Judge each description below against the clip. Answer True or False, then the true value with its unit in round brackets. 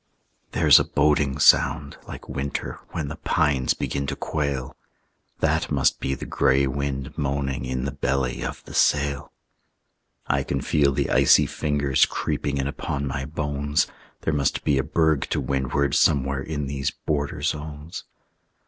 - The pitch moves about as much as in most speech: False (1.4 semitones)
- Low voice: True (70 Hz)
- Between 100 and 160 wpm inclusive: True (155 wpm)